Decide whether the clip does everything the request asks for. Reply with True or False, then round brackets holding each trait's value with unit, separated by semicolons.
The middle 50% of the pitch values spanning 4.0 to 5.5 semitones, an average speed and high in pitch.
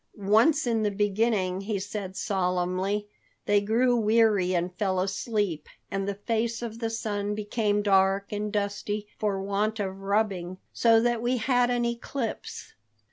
False (2.5 semitones; 150 wpm; 205 Hz)